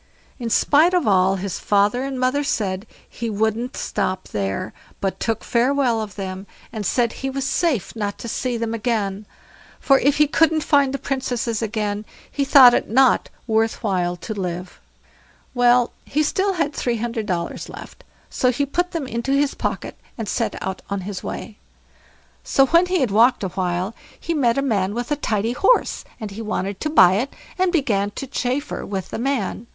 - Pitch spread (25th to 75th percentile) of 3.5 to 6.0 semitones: Yes, average, 5.1 semitones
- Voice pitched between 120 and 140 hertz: No, high, 235 Hz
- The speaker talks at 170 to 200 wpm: Yes, average, 190 wpm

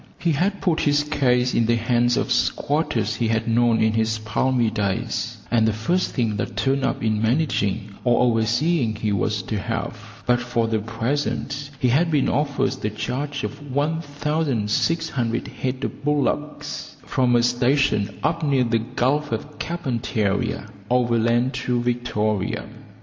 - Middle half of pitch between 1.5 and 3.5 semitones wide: No, average, 4.3 semitones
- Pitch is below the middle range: Yes, low, 120 Hz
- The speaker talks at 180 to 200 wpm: No, average, 155 wpm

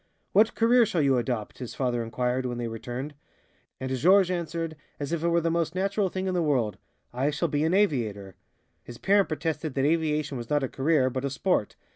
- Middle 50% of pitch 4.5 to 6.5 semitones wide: Yes, average, 5.2 semitones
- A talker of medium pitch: Yes, medium, 150 Hz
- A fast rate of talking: Yes, fast, 210 wpm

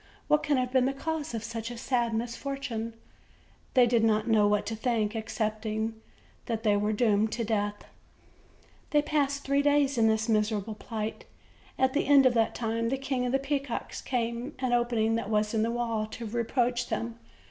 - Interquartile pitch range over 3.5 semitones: No, average, 3.0 semitones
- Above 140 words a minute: Yes, average, 190 wpm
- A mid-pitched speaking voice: No, high, 230 Hz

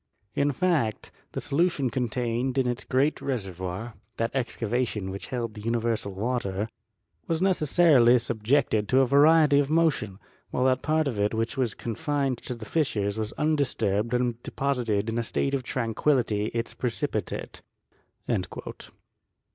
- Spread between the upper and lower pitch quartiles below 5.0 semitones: Yes, average, 4.1 semitones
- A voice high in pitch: No, low, 120 Hz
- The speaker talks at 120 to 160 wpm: Yes, average, 140 wpm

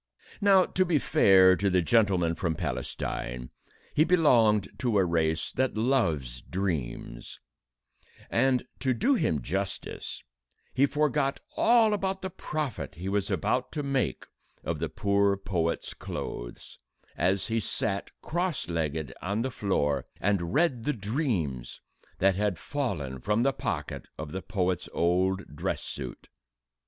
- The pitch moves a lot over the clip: Yes, wide, 8.0 semitones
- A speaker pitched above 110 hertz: No, low, 100 Hz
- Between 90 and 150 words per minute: Yes, slow, 135 wpm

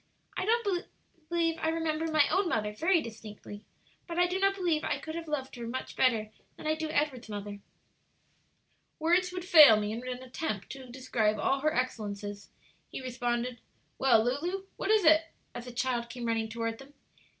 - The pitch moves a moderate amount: No, wide, 6.2 semitones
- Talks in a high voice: Yes, very high, 260 Hz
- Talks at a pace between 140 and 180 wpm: Yes, average, 175 wpm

